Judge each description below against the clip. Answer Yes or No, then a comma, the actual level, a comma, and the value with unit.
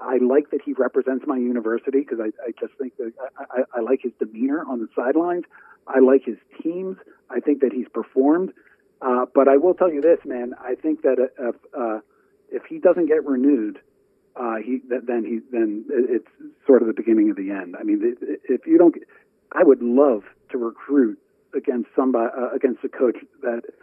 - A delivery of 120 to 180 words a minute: No, average, 200 wpm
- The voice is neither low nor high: Yes, medium, 180 Hz